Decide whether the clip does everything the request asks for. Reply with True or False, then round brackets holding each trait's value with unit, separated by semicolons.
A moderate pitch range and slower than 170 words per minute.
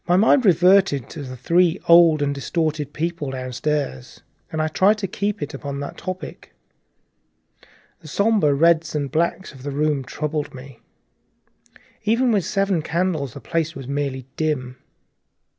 True (4.4 semitones; 155 wpm)